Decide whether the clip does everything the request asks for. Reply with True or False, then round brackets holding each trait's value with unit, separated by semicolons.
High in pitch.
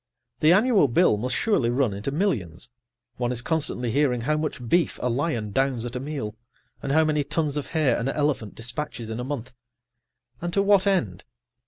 False (135 Hz)